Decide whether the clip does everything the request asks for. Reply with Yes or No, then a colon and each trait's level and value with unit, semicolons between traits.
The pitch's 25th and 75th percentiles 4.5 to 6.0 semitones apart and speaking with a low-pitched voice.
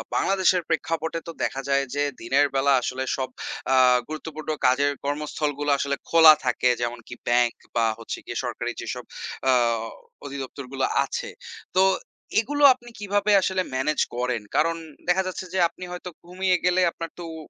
No: wide, 5.4 semitones; medium, 155 Hz